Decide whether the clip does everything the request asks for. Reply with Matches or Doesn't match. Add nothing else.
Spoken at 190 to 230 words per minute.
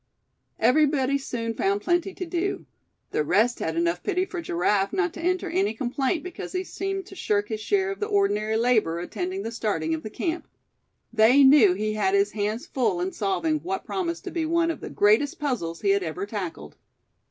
Matches